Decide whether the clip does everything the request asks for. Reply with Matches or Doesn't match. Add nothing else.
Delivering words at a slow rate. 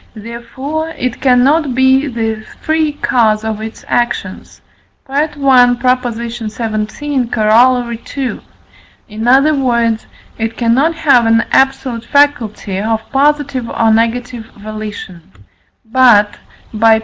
Matches